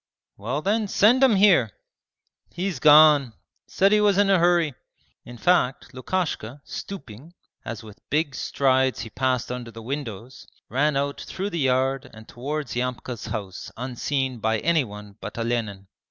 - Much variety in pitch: Yes, wide, 6.1 semitones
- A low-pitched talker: Yes, low, 130 Hz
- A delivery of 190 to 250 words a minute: No, average, 150 wpm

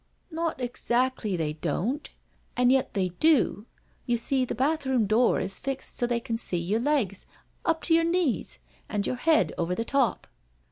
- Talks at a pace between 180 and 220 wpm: Yes, average, 185 wpm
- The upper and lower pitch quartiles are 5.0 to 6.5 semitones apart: Yes, average, 5.3 semitones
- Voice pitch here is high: Yes, high, 245 Hz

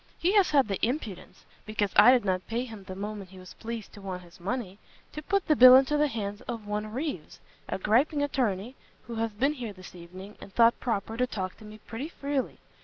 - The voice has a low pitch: No, high, 220 Hz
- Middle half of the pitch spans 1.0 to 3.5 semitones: No, average, 4.7 semitones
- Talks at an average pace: No, fast, 225 wpm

